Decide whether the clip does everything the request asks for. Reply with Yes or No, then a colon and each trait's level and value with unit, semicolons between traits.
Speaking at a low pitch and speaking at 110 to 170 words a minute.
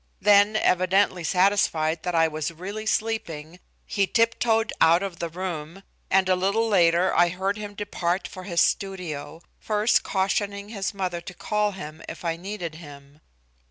No: medium, 185 Hz; average, 160 wpm